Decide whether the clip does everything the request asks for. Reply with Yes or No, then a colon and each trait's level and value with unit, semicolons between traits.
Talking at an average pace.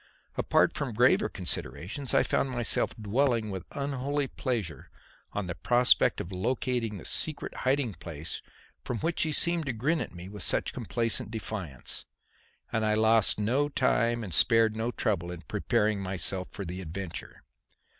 Yes: average, 155 wpm